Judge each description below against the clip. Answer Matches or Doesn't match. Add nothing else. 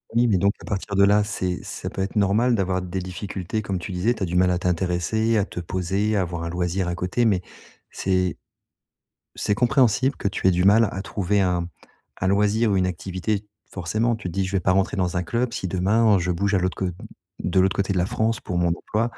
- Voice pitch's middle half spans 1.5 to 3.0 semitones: Matches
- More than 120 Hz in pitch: Doesn't match